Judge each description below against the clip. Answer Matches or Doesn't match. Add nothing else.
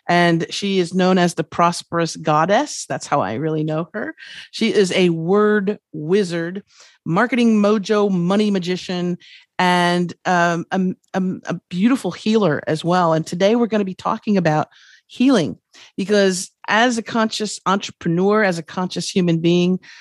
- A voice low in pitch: Doesn't match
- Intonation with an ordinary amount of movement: Matches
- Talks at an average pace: Matches